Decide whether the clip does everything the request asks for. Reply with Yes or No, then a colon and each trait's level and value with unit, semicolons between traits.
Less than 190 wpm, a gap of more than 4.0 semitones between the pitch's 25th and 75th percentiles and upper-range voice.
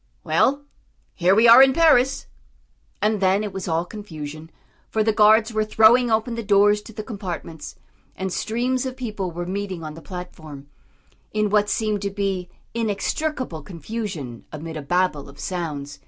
Yes: average, 165 wpm; average, 4.5 semitones; high, 200 Hz